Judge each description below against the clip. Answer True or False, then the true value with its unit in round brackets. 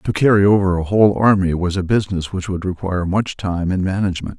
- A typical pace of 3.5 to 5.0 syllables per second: False (6.2 syllables/s)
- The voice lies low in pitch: True (95 Hz)